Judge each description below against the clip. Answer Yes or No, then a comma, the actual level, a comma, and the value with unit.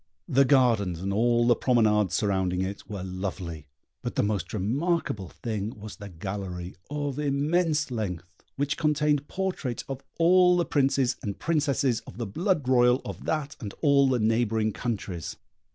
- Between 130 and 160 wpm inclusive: Yes, average, 155 wpm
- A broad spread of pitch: Yes, wide, 6.3 semitones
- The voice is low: Yes, low, 120 Hz